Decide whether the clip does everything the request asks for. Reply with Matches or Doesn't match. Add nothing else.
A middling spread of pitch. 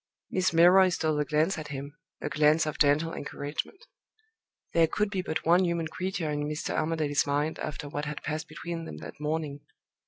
Doesn't match